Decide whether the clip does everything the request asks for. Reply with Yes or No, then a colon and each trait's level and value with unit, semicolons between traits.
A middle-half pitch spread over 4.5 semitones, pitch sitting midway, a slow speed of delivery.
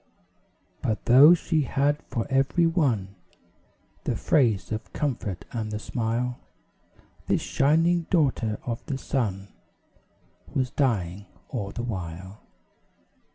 No: average, 5.2 semitones; low, 120 Hz; slow, 110 wpm